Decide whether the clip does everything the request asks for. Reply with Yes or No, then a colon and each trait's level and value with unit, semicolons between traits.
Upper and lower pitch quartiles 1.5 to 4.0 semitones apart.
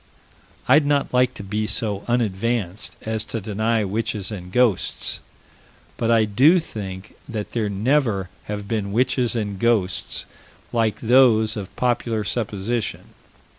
Yes: average, 2.9 semitones